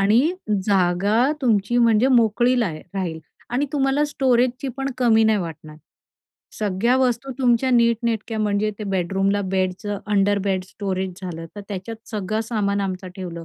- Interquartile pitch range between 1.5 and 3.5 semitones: No, average, 4.0 semitones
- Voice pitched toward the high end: Yes, high, 210 Hz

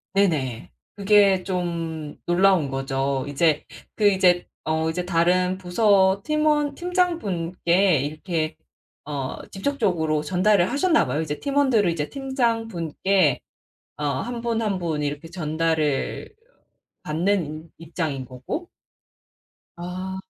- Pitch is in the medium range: Yes, medium, 175 Hz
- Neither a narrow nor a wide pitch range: Yes, average, 4.7 semitones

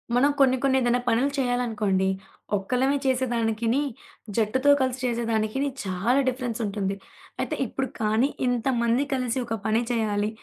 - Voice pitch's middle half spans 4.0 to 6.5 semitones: No, average, 3.0 semitones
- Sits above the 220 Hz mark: Yes, high, 240 Hz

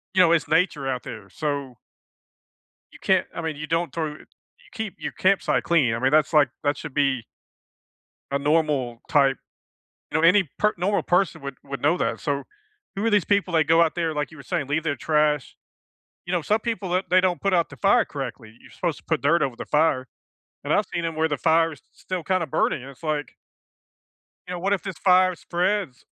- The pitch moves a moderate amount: Yes, average, 4.1 semitones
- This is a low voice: No, medium, 160 Hz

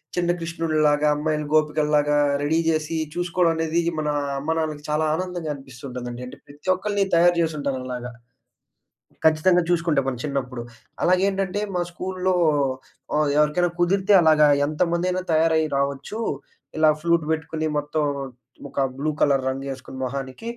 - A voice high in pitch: No, medium, 155 Hz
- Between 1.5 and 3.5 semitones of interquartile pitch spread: Yes, average, 3.1 semitones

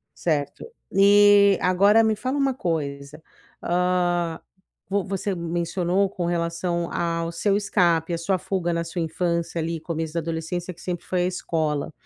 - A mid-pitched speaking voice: Yes, medium, 175 Hz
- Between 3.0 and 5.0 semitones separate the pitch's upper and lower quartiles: No, narrow, 2.4 semitones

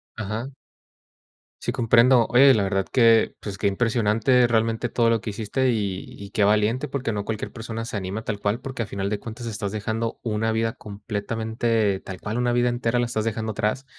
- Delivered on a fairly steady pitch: Yes, narrow, 2.3 semitones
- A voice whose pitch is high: No, low, 110 Hz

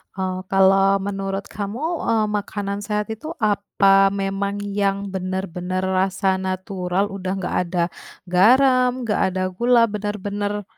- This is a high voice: Yes, high, 195 Hz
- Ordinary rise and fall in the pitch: No, narrow, 1.6 semitones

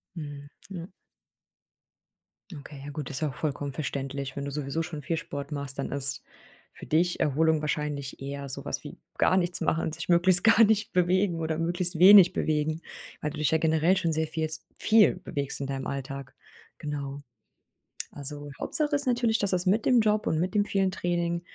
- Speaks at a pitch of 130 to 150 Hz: No, medium, 160 Hz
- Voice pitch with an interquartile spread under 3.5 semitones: No, average, 4.1 semitones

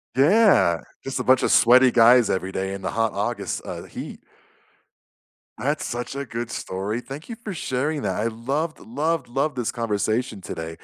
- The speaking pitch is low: Yes, low, 120 Hz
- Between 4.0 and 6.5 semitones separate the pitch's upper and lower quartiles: Yes, average, 4.6 semitones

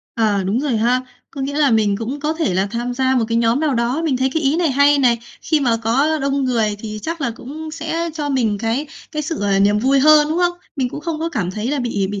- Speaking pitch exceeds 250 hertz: Yes, very high, 265 Hz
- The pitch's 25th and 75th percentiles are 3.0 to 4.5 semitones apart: No, average, 4.9 semitones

